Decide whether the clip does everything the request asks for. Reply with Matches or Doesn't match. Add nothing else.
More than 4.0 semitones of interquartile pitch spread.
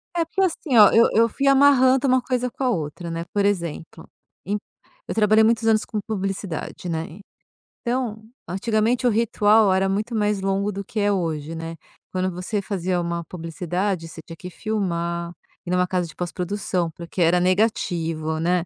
Matches